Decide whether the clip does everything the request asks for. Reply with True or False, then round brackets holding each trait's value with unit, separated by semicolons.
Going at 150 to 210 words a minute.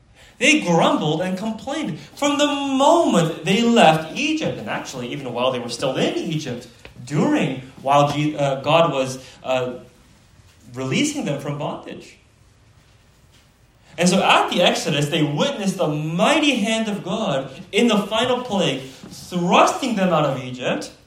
False (140 wpm)